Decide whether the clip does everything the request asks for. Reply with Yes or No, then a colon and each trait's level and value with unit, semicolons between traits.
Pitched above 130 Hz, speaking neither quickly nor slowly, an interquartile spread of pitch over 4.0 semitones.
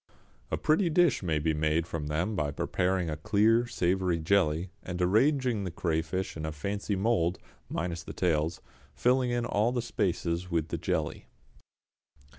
No: very low, 90 Hz; average, 155 wpm; average, 5.2 semitones